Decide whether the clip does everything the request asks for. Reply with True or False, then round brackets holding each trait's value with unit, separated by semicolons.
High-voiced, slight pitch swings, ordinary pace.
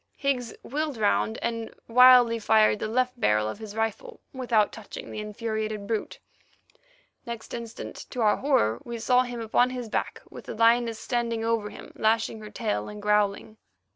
True (225 Hz; 2.3 semitones; 170 wpm)